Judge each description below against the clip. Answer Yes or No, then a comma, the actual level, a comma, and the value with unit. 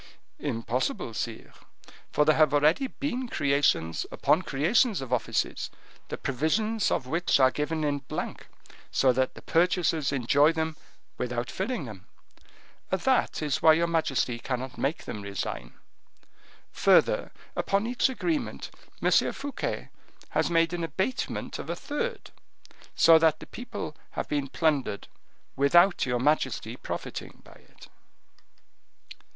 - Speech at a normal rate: No, slow, 130 wpm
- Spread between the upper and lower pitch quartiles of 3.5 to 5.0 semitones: No, wide, 5.4 semitones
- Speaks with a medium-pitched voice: Yes, medium, 155 Hz